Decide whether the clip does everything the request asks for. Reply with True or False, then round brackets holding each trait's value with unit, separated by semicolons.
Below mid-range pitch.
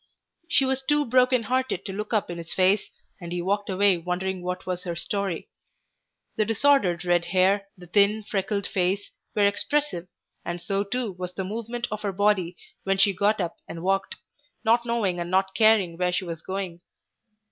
False (195 Hz)